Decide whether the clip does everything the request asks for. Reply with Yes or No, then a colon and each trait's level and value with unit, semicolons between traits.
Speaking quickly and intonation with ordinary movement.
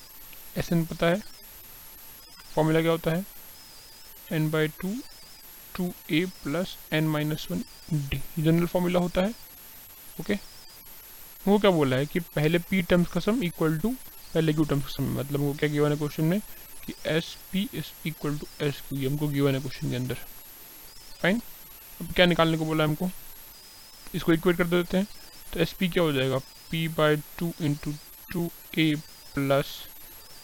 No: average, 175 wpm; average, 3.1 semitones